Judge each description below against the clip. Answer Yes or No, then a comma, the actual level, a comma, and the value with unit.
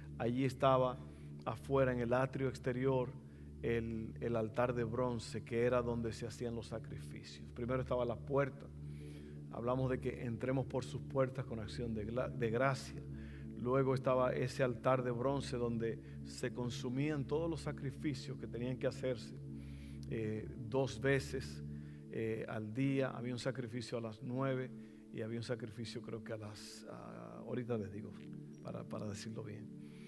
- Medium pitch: No, low, 120 Hz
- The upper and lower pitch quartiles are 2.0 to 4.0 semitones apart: Yes, average, 3.3 semitones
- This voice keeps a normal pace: Yes, average, 160 wpm